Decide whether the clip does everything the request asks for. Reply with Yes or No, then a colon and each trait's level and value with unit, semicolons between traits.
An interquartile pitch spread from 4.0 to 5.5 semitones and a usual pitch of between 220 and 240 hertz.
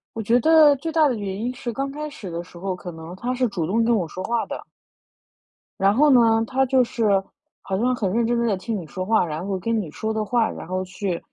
Yes: average, 4.9 semitones; high, 225 Hz